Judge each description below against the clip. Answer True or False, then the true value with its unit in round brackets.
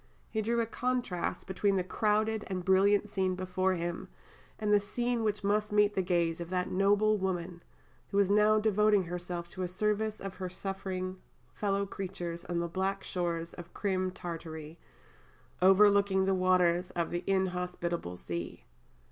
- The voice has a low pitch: False (190 Hz)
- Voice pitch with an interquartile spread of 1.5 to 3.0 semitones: True (2.7 semitones)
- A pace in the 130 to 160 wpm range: True (155 wpm)